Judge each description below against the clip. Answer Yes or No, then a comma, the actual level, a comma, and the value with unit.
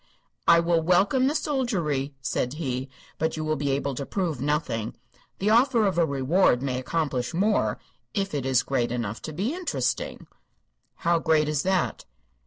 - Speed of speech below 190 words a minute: Yes, average, 170 wpm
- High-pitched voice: No, medium, 155 Hz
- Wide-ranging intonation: Yes, wide, 6.0 semitones